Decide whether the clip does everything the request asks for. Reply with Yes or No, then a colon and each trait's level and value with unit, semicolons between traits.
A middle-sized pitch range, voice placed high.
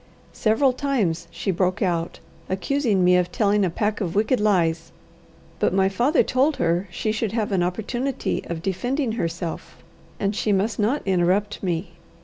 Yes: average, 4.0 semitones; high, 200 Hz